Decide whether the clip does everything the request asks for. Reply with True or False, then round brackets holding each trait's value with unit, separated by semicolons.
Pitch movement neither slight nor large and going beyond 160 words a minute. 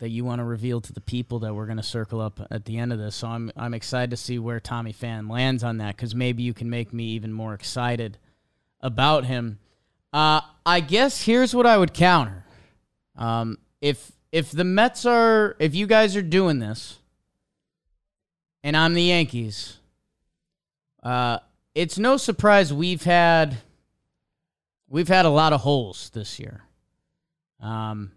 False (6.5 semitones; 175 wpm)